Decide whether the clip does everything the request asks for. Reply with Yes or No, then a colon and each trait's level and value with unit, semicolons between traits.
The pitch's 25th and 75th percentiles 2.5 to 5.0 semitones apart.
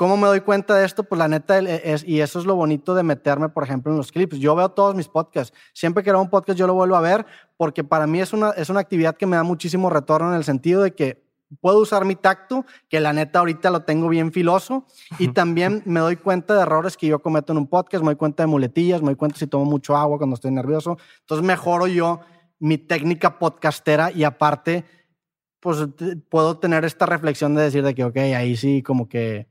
Yes: average, 3.4 semitones